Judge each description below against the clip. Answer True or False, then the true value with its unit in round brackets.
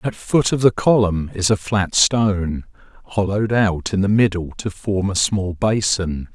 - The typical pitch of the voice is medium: False (100 Hz)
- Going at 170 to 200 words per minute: True (180 wpm)